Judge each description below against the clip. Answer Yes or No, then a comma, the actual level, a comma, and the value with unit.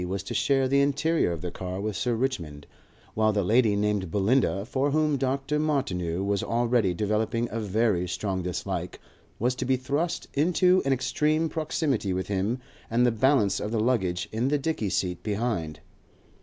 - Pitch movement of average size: No, wide, 5.7 semitones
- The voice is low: Yes, low, 115 Hz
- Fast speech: No, average, 175 wpm